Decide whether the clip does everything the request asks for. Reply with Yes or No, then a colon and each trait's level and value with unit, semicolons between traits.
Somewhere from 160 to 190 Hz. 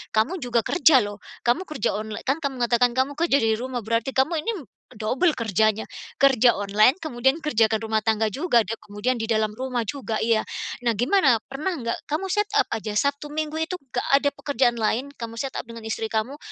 No: high, 240 Hz